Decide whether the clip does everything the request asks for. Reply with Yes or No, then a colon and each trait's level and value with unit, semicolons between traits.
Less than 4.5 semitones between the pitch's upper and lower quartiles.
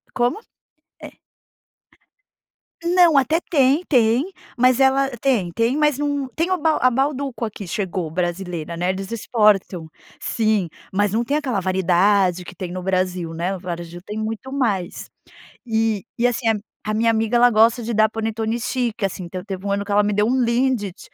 No: average, 5.0 semitones